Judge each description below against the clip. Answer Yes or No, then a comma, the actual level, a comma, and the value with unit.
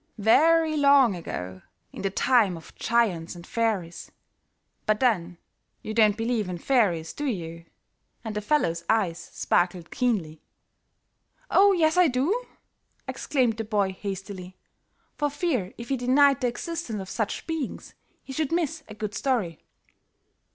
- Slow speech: No, average, 145 wpm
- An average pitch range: No, wide, 6.9 semitones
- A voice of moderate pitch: No, high, 225 Hz